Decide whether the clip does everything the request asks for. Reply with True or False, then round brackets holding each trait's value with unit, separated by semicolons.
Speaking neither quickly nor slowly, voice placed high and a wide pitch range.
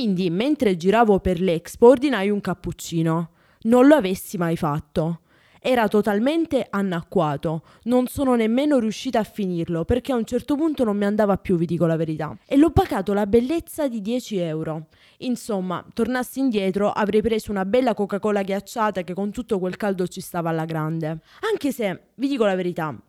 False (175 wpm; 205 Hz; 6.0 semitones)